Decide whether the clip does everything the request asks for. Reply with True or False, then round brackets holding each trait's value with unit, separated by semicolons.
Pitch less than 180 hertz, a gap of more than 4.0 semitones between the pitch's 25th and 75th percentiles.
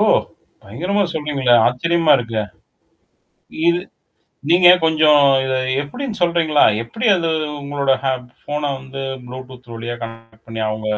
True (135 Hz; 5.3 semitones)